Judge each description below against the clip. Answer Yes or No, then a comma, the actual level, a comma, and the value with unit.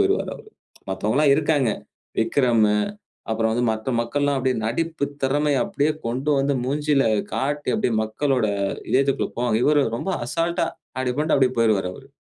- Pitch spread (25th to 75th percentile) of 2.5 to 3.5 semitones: No, average, 4.0 semitones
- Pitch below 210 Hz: Yes, low, 135 Hz